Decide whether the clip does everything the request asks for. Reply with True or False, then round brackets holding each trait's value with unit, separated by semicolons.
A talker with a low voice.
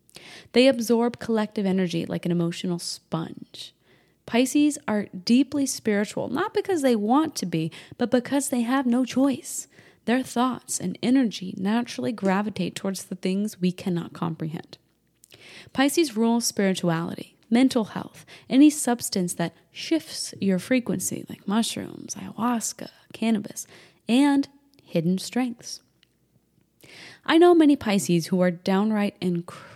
False (225 Hz)